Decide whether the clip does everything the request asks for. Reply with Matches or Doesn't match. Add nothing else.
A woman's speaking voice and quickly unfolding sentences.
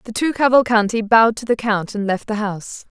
Matches